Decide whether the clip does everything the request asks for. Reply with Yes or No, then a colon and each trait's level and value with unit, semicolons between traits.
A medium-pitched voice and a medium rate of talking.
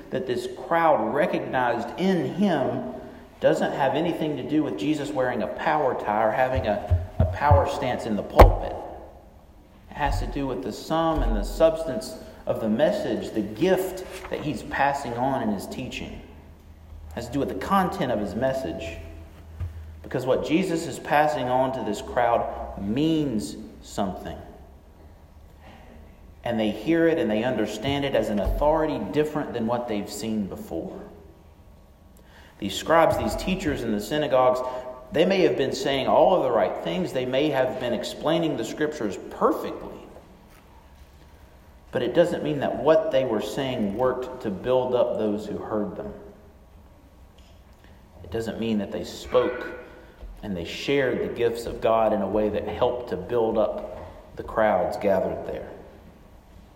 No: low, 110 Hz; average, 160 wpm